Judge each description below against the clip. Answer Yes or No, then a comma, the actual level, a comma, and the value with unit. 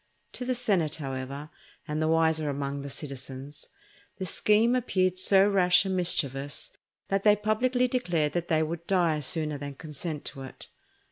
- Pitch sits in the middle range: Yes, medium, 160 Hz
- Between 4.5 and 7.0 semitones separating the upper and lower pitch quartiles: Yes, average, 5.3 semitones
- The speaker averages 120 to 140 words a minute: No, average, 155 wpm